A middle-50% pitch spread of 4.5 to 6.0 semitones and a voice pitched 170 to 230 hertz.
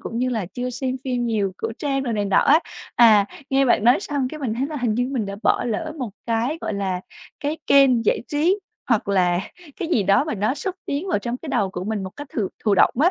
No: average, 5.1 semitones; high, 240 Hz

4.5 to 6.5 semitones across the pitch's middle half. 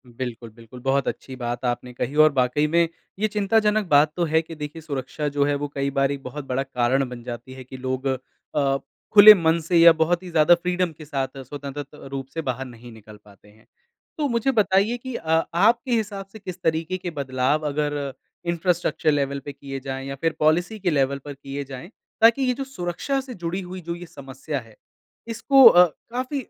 Yes: average, 5.0 semitones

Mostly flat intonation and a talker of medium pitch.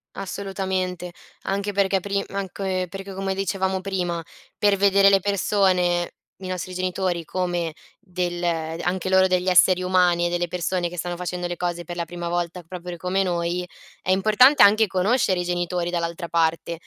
Yes: narrow, 1.7 semitones; medium, 180 Hz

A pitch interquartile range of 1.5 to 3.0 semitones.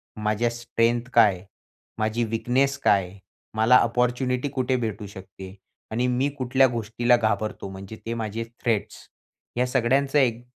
Yes: average, 2.7 semitones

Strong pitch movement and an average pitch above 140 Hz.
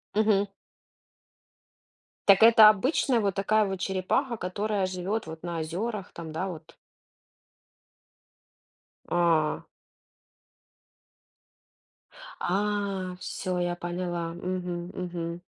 No: average, 2.9 semitones; medium, 185 Hz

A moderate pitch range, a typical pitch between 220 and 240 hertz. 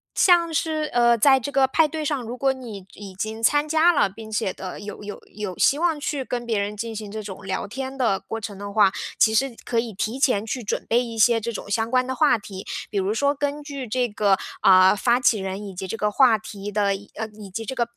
Yes: average, 4.5 semitones; high, 225 Hz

